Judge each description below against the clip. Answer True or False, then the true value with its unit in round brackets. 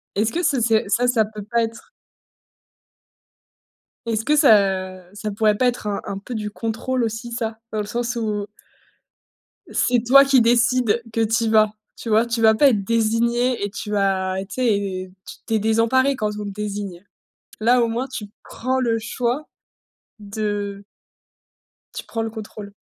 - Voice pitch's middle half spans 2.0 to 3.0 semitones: True (2.4 semitones)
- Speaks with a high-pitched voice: True (225 Hz)